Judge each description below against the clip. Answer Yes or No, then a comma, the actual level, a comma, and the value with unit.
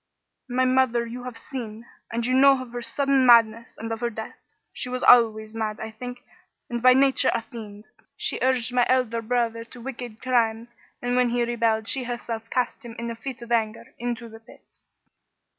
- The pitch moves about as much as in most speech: No, narrow, 1.7 semitones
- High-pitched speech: Yes, high, 235 Hz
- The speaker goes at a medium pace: Yes, average, 195 wpm